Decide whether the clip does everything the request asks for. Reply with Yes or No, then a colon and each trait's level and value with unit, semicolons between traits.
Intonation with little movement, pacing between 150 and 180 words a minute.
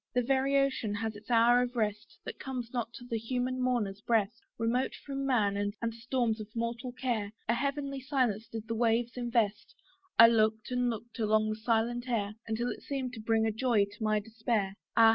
No: narrow, 2.3 semitones; average, 200 wpm